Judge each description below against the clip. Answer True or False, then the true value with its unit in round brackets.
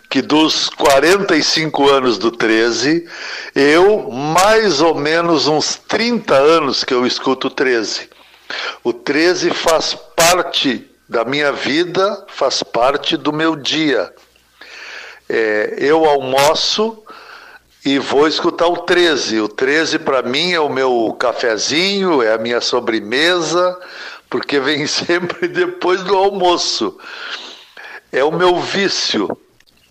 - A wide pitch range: True (6.4 semitones)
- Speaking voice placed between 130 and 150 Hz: False (175 Hz)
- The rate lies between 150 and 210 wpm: False (120 wpm)